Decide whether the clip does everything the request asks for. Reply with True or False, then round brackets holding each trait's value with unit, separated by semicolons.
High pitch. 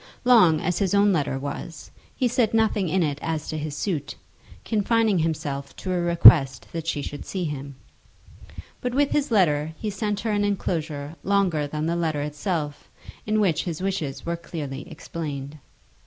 False (165 Hz)